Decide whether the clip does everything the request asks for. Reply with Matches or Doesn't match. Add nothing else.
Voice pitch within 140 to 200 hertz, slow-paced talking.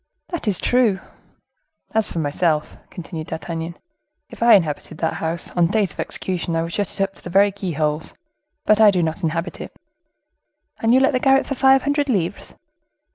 Doesn't match